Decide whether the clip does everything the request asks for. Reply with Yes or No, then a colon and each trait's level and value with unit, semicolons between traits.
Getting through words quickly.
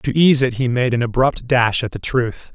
Yes: fast, 260 wpm